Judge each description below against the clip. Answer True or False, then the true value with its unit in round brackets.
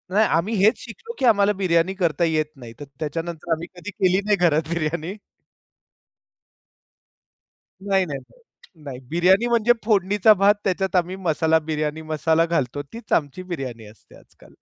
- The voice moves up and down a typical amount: True (4.1 semitones)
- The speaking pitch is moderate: True (170 Hz)